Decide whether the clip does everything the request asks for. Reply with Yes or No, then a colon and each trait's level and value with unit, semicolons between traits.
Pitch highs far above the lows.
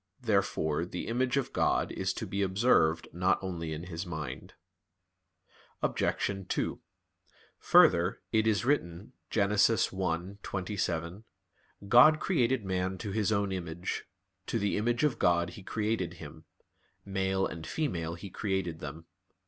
No: average, 4.1 semitones